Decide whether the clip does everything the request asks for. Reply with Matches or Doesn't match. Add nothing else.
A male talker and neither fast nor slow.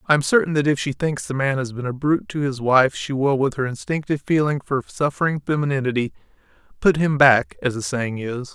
Doesn't match